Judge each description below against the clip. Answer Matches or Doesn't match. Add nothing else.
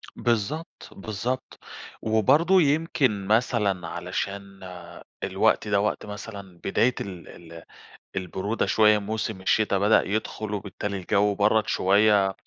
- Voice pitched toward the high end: Doesn't match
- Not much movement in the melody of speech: Matches